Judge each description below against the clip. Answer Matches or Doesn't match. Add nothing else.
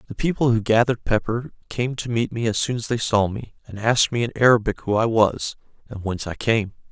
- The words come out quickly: Matches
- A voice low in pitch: Matches